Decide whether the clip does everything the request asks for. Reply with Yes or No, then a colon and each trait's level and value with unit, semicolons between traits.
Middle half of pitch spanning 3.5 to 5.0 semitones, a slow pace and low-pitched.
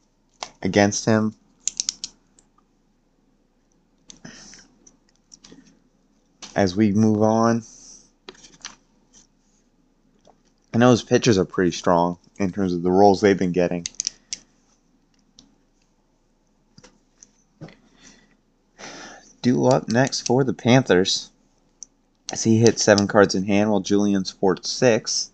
Yes: average, 3.9 semitones; slow, 90 wpm; low, 105 Hz